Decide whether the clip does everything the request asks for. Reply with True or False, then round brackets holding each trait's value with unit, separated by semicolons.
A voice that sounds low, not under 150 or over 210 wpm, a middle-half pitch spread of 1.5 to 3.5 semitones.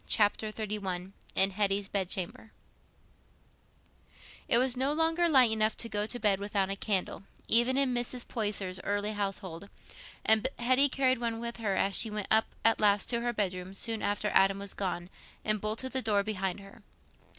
False (210 Hz; 175 wpm; 3.1 semitones)